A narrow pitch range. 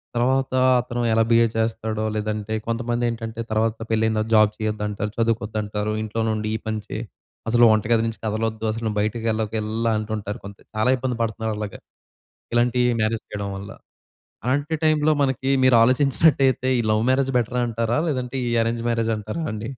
Yes: narrow, 1.8 semitones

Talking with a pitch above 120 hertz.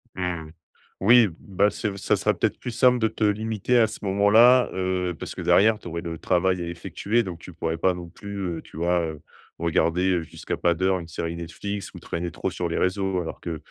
No: very low, 95 Hz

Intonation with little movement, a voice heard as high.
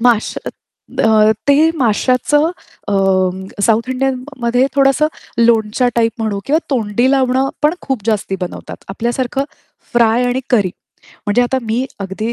No: average, 3.2 semitones; high, 240 Hz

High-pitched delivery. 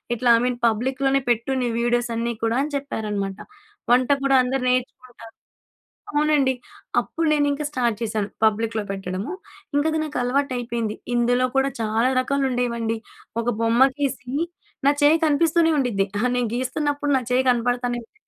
Yes: high, 245 Hz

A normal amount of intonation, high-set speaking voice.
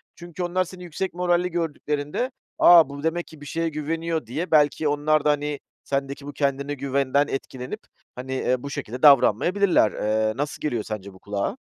No: average, 3.7 semitones; medium, 145 Hz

